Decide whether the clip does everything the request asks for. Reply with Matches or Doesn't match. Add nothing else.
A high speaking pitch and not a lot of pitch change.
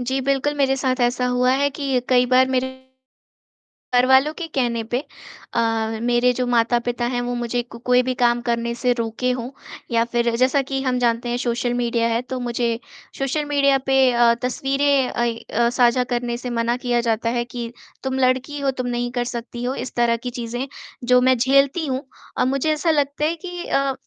Matches